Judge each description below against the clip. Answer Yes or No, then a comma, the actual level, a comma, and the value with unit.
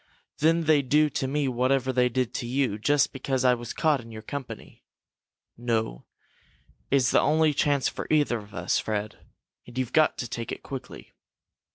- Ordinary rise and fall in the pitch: Yes, average, 3.4 semitones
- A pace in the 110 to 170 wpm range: No, average, 180 wpm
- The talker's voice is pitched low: Yes, low, 130 Hz